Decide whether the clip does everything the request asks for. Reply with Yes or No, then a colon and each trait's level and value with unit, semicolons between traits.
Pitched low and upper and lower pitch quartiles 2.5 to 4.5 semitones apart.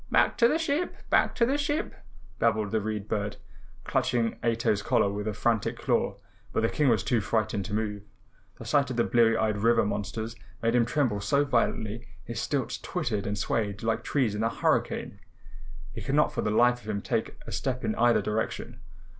Yes: low, 115 Hz; average, 2.8 semitones